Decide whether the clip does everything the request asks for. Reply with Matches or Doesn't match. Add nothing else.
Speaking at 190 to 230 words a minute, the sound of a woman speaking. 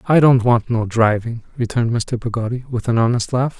Doesn't match